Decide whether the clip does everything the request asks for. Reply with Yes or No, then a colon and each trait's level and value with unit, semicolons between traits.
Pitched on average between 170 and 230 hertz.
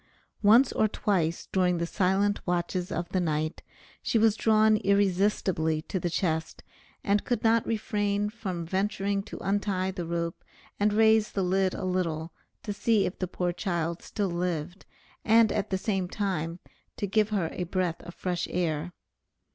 Yes: high, 190 Hz